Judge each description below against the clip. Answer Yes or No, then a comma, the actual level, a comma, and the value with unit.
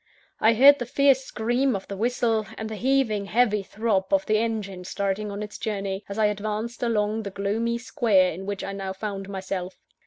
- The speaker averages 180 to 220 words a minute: Yes, average, 195 wpm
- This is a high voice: Yes, high, 215 Hz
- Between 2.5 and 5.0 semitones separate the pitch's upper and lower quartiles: Yes, average, 2.9 semitones